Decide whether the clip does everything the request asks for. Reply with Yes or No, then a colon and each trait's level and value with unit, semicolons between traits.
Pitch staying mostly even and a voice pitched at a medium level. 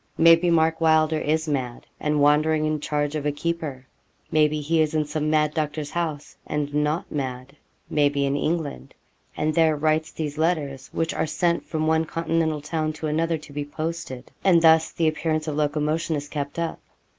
Yes: narrow, 1.6 semitones; medium, 155 Hz